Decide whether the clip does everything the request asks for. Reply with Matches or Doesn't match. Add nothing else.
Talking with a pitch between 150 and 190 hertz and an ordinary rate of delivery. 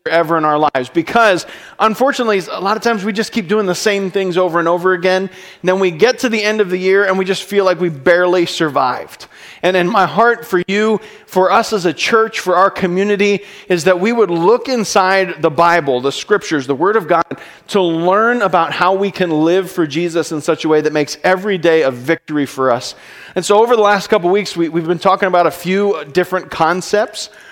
Doesn't match